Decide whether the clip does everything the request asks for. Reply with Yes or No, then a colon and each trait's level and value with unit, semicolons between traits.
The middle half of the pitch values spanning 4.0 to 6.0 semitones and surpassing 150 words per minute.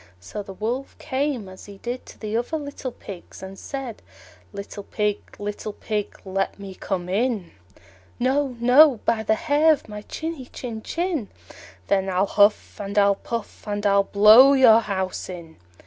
Yes: average, 4.5 semitones; average, 165 wpm